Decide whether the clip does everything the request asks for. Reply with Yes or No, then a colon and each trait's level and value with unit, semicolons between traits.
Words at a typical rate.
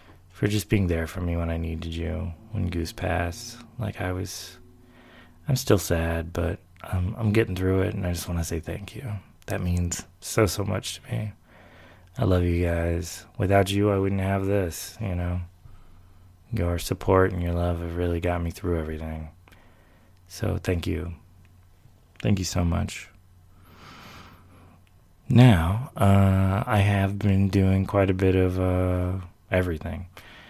Yes: average, 160 wpm